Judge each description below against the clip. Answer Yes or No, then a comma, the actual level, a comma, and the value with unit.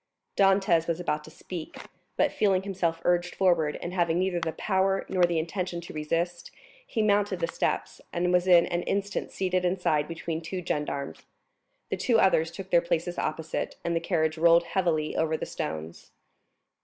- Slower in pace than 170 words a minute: No, average, 175 wpm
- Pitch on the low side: No, medium, 175 Hz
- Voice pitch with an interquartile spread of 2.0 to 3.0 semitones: Yes, narrow, 2.5 semitones